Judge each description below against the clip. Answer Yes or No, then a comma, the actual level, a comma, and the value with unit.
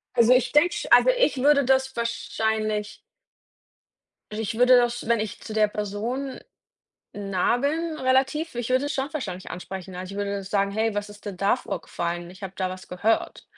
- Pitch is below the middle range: No, high, 220 Hz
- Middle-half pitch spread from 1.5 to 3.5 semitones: No, average, 4.7 semitones